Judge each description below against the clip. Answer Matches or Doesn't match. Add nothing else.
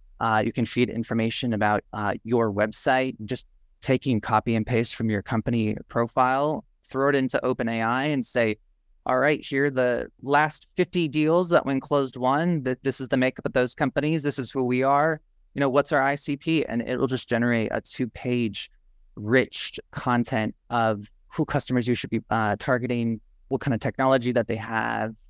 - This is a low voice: Matches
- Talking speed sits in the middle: Matches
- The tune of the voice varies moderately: Matches